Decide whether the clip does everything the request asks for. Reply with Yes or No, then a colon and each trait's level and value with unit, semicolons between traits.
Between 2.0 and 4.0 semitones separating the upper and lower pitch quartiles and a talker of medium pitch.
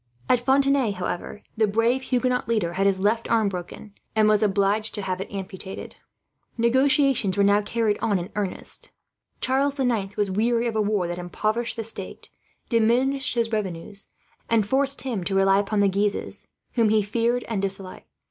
No: average, 3.2 semitones; high, 215 Hz